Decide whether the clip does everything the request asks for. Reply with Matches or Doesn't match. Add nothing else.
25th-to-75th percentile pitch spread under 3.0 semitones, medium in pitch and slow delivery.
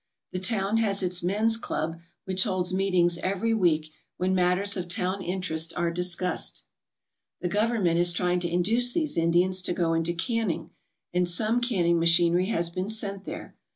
Doesn't match